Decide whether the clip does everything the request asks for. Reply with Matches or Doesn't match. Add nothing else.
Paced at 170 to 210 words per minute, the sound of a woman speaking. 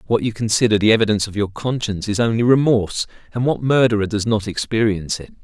Doesn't match